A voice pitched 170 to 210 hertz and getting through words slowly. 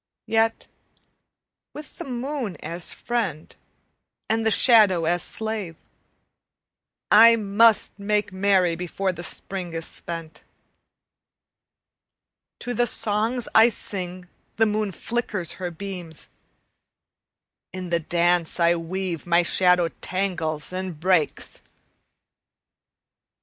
Yes: medium, 185 Hz; slow, 100 wpm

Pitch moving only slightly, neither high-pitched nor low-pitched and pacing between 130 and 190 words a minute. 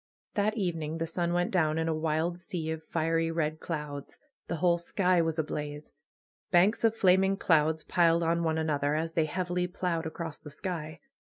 Yes: narrow, 2.0 semitones; medium, 165 Hz; average, 180 wpm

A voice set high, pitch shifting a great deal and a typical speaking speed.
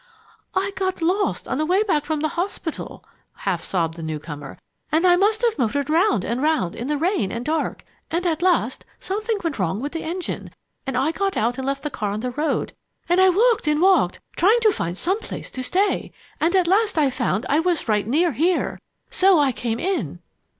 No: very high, 315 Hz; wide, 7.2 semitones; fast, 215 wpm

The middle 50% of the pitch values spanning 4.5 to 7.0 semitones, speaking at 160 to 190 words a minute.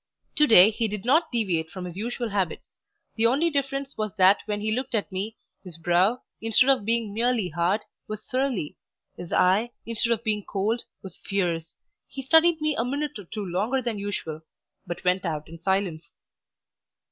Yes: average, 4.8 semitones; average, 180 wpm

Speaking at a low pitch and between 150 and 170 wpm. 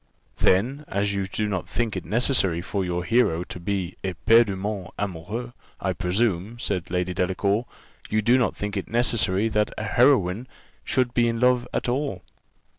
Yes: low, 105 Hz; average, 165 wpm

